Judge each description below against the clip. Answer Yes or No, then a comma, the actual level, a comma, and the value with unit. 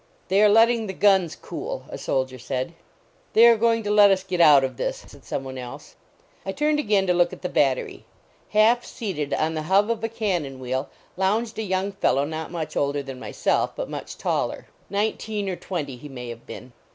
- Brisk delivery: Yes, fast, 210 wpm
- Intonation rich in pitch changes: Yes, wide, 7.1 semitones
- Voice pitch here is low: No, medium, 185 Hz